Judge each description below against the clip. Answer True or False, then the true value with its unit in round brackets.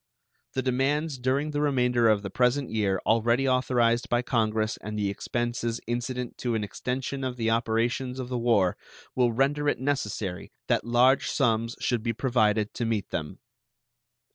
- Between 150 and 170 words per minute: True (165 wpm)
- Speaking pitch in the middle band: False (120 Hz)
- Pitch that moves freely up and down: False (2.5 semitones)